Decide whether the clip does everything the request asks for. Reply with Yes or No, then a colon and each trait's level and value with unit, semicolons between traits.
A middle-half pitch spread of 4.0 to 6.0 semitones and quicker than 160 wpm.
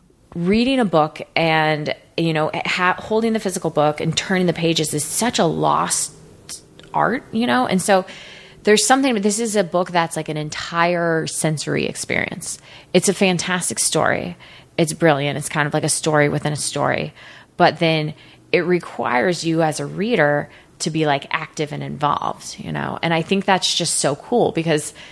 No: average, 3.5 semitones; average, 180 wpm